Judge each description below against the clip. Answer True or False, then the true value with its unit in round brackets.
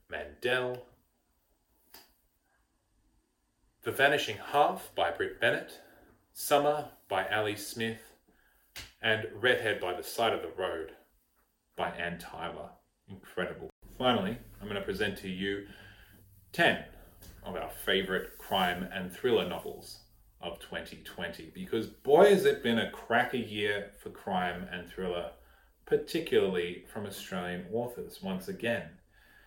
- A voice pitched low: True (100 Hz)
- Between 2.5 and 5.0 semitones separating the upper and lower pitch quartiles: False (5.5 semitones)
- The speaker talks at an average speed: False (120 wpm)